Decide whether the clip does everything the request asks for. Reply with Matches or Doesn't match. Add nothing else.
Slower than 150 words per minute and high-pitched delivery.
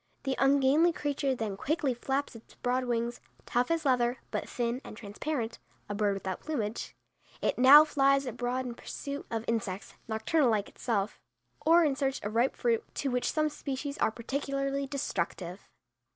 Doesn't match